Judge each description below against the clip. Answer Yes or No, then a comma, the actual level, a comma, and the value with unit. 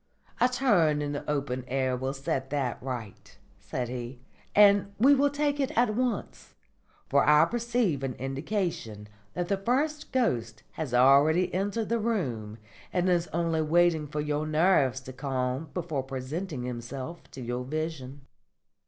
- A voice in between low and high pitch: Yes, medium, 150 Hz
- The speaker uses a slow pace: No, average, 155 wpm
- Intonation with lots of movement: Yes, wide, 7.1 semitones